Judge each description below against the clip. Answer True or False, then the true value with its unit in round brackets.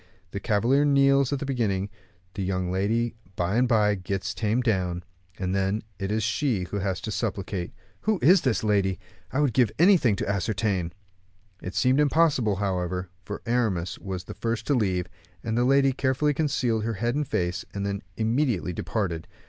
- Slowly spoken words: False (175 wpm)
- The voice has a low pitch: True (110 Hz)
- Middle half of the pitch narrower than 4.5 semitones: False (5.0 semitones)